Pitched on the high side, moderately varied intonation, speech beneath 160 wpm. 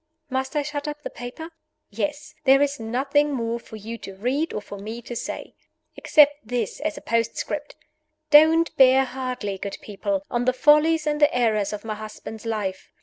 No: very high, 255 Hz; average, 5.0 semitones; average, 185 wpm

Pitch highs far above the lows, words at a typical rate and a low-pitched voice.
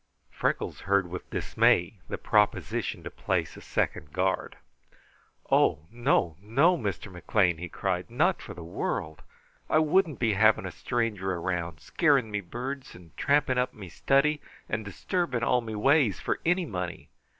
Yes: wide, 7.0 semitones; average, 155 wpm; low, 105 Hz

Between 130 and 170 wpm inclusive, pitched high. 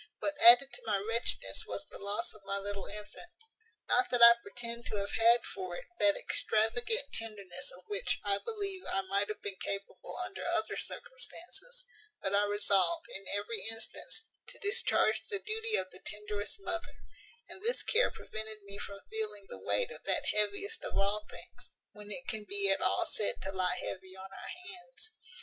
No: average, 185 wpm; high, 215 Hz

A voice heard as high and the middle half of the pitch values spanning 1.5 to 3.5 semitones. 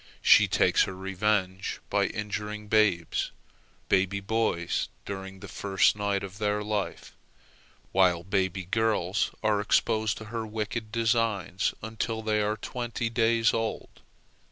No: low, 105 Hz; narrow, 2.5 semitones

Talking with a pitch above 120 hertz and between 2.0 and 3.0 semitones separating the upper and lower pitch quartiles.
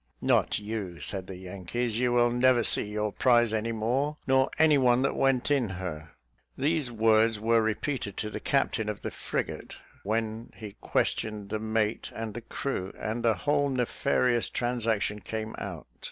No: low, 115 Hz; average, 2.7 semitones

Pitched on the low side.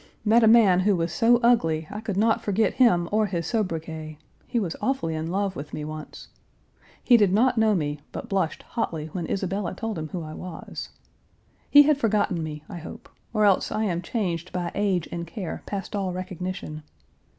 No: medium, 185 Hz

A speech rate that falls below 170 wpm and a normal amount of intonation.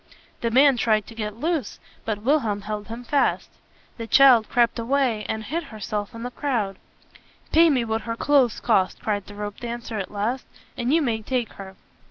No: average, 185 wpm; average, 3.5 semitones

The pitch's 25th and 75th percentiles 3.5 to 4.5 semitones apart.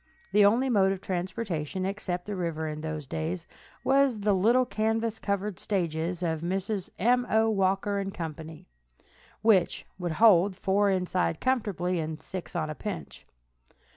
Yes: average, 3.8 semitones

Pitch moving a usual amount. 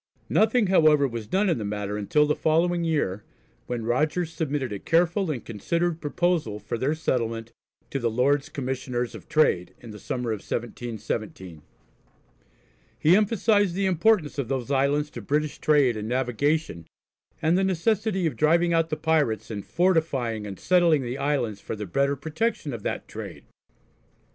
No: wide, 6.1 semitones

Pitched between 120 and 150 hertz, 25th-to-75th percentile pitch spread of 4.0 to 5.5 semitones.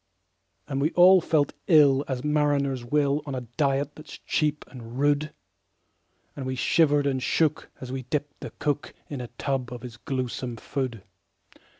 No: medium, 140 Hz; narrow, 2.4 semitones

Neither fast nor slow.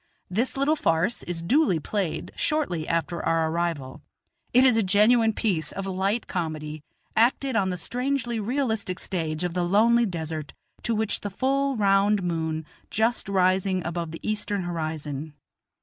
Yes: average, 150 wpm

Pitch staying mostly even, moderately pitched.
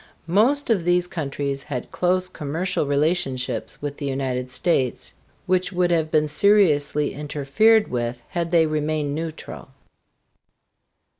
No: average, 4.1 semitones; medium, 155 Hz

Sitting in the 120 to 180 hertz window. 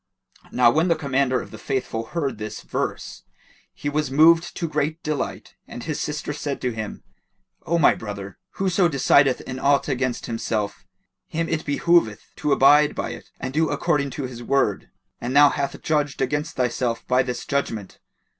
Yes: medium, 140 Hz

